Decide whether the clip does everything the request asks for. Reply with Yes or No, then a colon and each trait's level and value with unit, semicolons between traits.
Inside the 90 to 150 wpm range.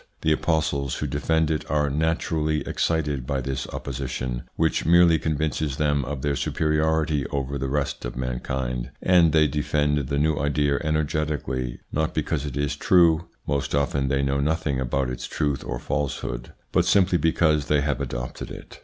No: average, 165 wpm